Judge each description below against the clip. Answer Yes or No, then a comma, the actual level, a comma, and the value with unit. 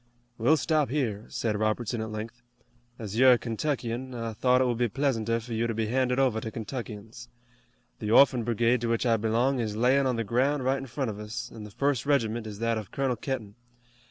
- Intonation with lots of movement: No, average, 2.8 semitones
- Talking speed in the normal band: No, fast, 215 wpm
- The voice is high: No, low, 115 Hz